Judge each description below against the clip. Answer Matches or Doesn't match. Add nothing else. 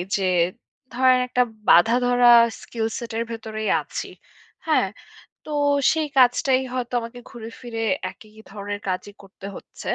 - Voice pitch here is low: Doesn't match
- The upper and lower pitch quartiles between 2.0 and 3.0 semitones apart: Matches